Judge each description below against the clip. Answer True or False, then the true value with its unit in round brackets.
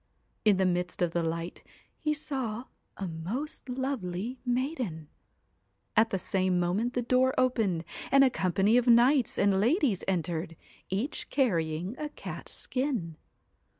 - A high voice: True (215 Hz)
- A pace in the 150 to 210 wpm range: False (140 wpm)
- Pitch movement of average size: False (6.3 semitones)